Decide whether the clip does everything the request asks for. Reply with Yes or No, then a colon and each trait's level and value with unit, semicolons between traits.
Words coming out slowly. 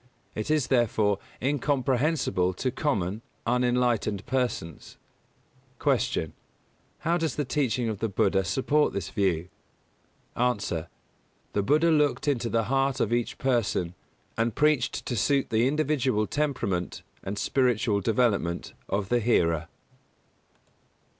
Yes: slow, 120 wpm